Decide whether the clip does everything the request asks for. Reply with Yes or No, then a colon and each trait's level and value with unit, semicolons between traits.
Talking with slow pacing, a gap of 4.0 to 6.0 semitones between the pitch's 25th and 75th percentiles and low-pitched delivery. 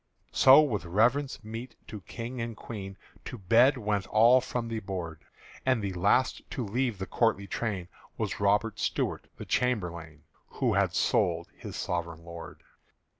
No: average, 155 wpm; average, 4.3 semitones; low, 110 Hz